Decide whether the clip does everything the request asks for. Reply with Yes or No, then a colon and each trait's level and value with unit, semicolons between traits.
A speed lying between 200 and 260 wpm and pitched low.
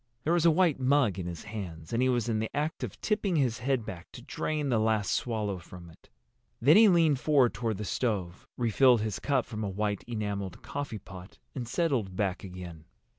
Yes: fast, 205 wpm; low, 110 Hz